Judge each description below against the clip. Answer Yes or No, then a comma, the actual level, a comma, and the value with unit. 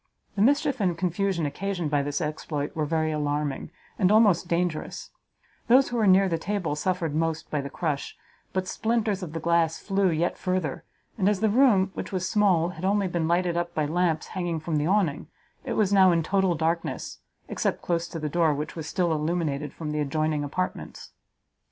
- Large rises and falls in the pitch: No, average, 3.7 semitones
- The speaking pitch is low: No, medium, 170 Hz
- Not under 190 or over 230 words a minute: Yes, average, 195 wpm